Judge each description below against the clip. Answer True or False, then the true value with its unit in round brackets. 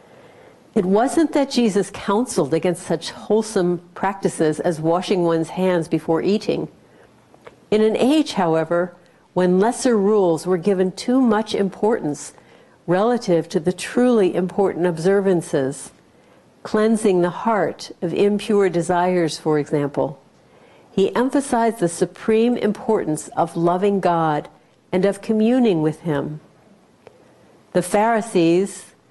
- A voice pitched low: False (185 Hz)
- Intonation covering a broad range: False (4.1 semitones)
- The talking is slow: True (115 wpm)